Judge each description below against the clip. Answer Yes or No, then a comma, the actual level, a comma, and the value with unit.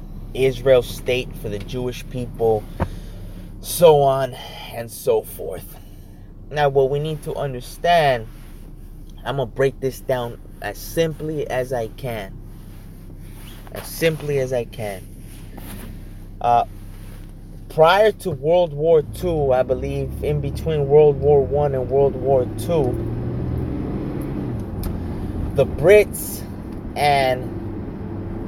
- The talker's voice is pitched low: Yes, low, 125 Hz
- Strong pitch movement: Yes, wide, 5.8 semitones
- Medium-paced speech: No, slow, 110 wpm